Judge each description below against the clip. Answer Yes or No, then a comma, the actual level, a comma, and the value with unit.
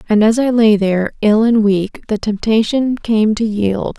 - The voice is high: Yes, high, 215 Hz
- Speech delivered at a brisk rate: No, average, 195 wpm